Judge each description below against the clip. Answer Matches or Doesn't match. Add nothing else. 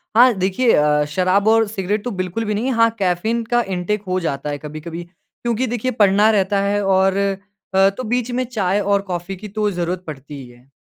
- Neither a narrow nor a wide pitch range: Matches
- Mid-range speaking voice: Doesn't match